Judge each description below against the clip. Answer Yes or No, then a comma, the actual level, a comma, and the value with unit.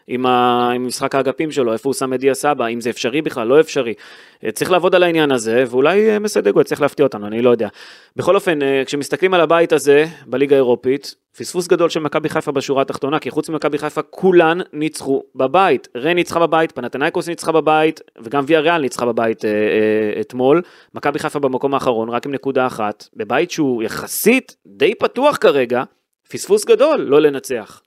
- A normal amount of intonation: Yes, average, 4.6 semitones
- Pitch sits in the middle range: Yes, medium, 145 Hz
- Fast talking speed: Yes, fast, 175 wpm